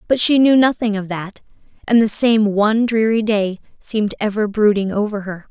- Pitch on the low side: No, high, 215 Hz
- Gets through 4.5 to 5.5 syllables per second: Yes, 5.2 syllables/s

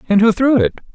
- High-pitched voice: Yes, high, 205 Hz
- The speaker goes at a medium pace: No, fast, 255 wpm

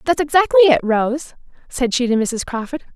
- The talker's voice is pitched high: Yes, very high, 270 Hz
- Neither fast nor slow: Yes, average, 185 wpm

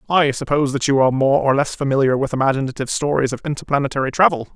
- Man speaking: Yes, male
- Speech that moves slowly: No, average, 200 wpm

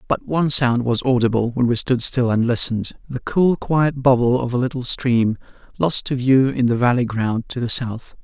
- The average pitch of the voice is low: Yes, low, 125 Hz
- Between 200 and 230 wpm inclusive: Yes, fast, 205 wpm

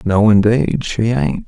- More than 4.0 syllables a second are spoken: No, 3.5 syllables/s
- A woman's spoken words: No, male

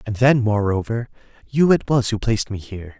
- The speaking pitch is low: Yes, low, 110 Hz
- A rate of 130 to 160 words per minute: No, average, 200 wpm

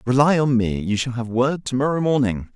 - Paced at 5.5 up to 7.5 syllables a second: No, 4.9 syllables/s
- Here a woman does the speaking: No, male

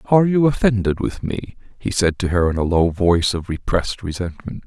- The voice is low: Yes, low, 100 Hz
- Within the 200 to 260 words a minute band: Yes, fast, 205 wpm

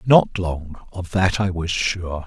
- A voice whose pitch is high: No, very low, 90 Hz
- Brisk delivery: No, average, 185 wpm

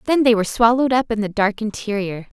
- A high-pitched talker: Yes, high, 220 Hz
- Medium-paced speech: No, fast, 225 wpm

